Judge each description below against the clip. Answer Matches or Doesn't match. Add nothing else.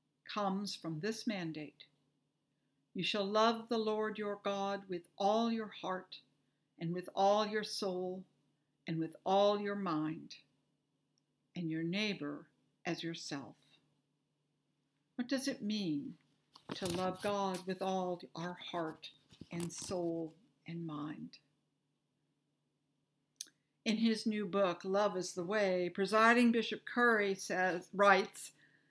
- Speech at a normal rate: Doesn't match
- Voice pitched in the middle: Matches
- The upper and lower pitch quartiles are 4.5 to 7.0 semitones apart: Matches